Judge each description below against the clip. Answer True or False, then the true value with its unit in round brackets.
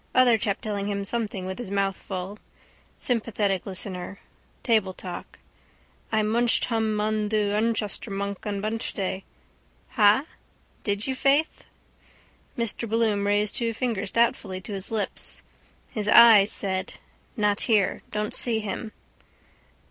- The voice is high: True (210 Hz)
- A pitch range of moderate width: False (2.3 semitones)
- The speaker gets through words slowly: True (130 wpm)